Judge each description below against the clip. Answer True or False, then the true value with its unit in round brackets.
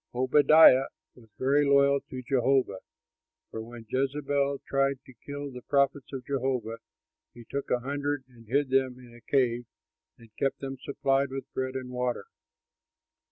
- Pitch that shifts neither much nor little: False (2.0 semitones)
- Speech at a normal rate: True (155 wpm)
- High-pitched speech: False (135 Hz)